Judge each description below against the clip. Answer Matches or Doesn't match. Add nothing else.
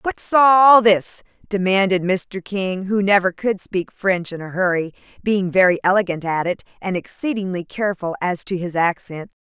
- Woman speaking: Matches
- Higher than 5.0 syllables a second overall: Doesn't match